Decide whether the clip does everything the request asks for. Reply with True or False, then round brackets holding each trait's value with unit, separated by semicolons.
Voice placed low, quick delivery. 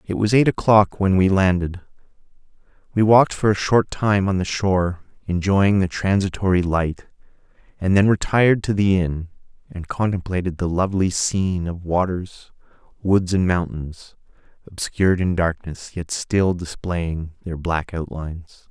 False (90 Hz; 145 wpm)